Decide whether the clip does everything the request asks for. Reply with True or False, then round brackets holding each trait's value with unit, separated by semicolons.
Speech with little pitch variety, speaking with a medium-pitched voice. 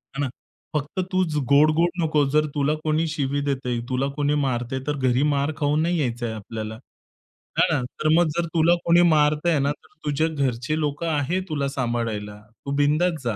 False (3.1 semitones; 145 Hz)